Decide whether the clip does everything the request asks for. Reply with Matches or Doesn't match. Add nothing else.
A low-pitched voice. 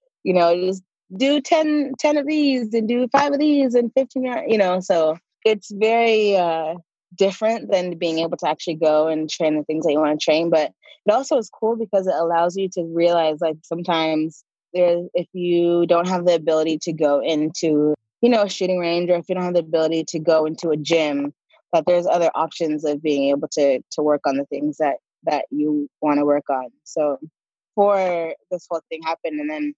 Doesn't match